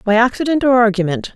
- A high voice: Yes, high, 230 Hz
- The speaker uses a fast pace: No, average, 175 wpm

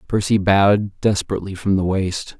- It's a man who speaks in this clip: Yes, male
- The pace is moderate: Yes, average, 150 wpm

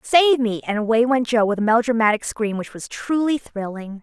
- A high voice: Yes, high, 230 Hz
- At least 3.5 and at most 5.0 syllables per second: No, 5.4 syllables/s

